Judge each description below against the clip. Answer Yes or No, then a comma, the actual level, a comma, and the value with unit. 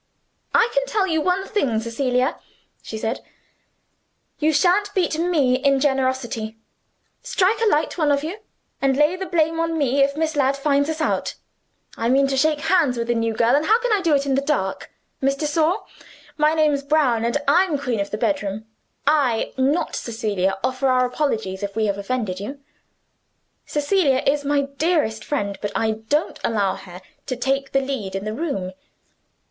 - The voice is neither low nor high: No, very high, 275 Hz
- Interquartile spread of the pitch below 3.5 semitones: No, average, 5.2 semitones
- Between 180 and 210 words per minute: Yes, average, 185 wpm